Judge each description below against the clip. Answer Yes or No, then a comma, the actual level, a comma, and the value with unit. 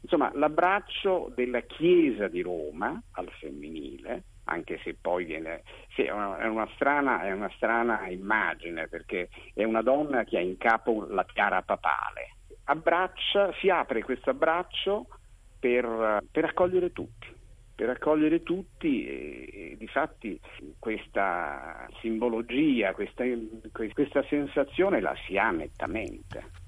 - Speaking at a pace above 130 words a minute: No, average, 125 wpm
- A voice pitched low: Yes, low, 125 Hz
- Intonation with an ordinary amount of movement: No, wide, 8.5 semitones